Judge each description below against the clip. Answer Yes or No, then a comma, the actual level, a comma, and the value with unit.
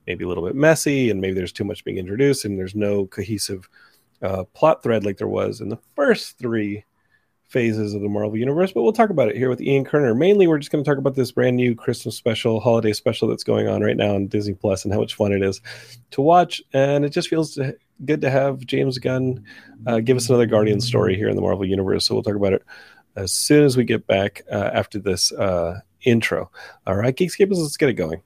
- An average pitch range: Yes, average, 5.0 semitones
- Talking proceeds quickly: Yes, fast, 240 wpm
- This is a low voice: Yes, low, 120 Hz